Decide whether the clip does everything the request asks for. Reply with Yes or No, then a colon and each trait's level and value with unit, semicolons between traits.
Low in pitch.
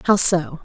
No: medium, 170 Hz